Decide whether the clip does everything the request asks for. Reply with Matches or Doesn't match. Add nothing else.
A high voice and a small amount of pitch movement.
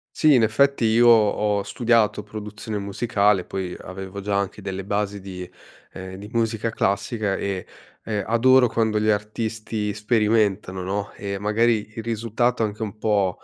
Doesn't match